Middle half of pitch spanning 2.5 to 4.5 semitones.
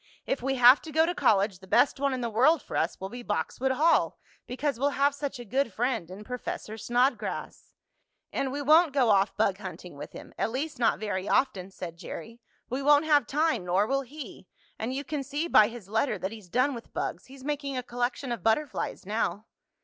No: average, 5.0 semitones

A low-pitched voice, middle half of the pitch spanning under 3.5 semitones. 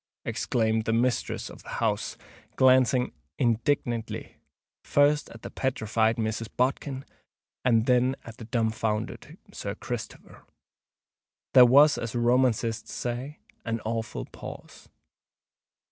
Yes: low, 120 Hz; narrow, 2.4 semitones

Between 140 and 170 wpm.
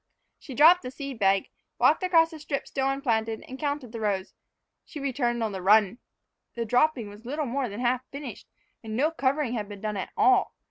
No: average, 200 wpm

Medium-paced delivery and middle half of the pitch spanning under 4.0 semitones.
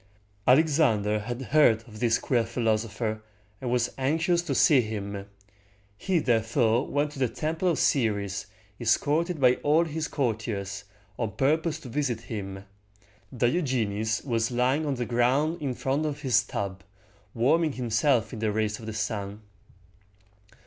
No: average, 145 wpm; average, 4.9 semitones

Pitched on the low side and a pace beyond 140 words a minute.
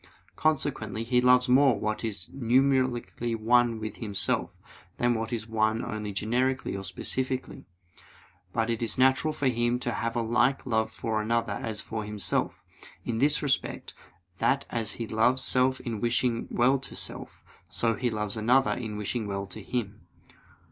Yes: low, 115 Hz; average, 160 wpm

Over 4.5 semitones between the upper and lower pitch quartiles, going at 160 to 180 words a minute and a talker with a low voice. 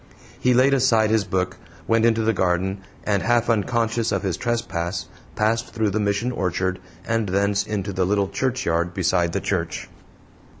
No: average, 3.5 semitones; average, 165 wpm; low, 105 Hz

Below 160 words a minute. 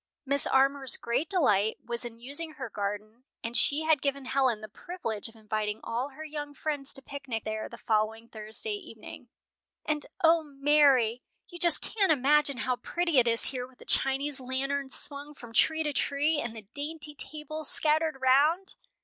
No: average, 175 wpm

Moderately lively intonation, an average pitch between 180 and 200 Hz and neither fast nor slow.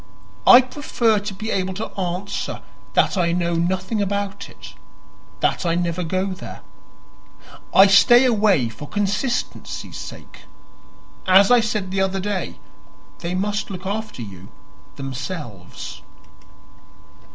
No: average, 3.1 semitones; high, 190 Hz; slow, 125 wpm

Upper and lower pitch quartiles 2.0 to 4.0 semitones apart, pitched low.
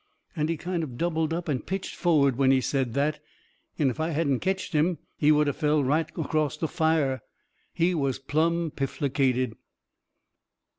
No: average, 3.1 semitones; medium, 150 Hz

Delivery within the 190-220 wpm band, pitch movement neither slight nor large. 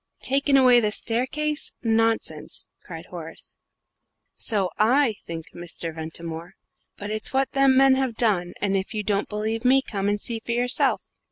No: average, 160 wpm; average, 4.6 semitones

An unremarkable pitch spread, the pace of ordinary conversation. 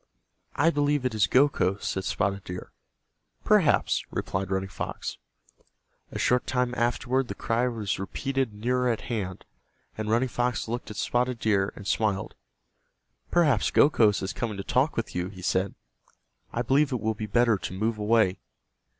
Yes: average, 4.1 semitones; average, 160 wpm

